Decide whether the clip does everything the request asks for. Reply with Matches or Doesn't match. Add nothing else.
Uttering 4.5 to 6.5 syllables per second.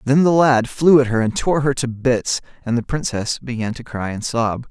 Matches